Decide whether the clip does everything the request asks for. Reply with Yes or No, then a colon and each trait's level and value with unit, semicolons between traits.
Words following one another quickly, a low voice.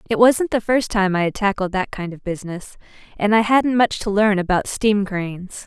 No: fast, 220 wpm; high, 205 Hz